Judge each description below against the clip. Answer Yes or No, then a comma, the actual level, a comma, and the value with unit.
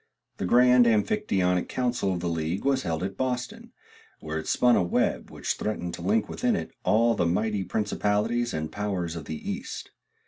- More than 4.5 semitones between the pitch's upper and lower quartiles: Yes, wide, 5.5 semitones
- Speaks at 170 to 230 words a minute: Yes, average, 180 wpm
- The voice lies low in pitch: Yes, low, 105 Hz